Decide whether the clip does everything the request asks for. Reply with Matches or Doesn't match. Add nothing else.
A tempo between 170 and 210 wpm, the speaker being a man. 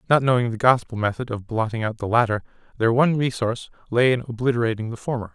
Matches